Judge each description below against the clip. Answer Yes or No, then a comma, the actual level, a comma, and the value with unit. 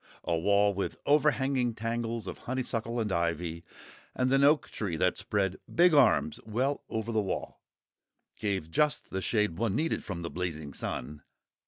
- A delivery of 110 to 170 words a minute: Yes, average, 160 wpm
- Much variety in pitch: Yes, wide, 6.1 semitones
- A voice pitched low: Yes, low, 110 Hz